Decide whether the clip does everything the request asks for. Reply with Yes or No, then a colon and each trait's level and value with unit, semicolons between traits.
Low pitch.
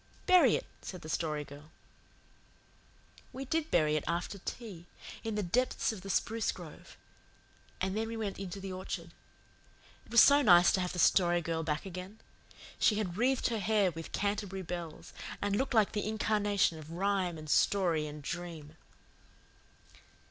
No: high, 190 Hz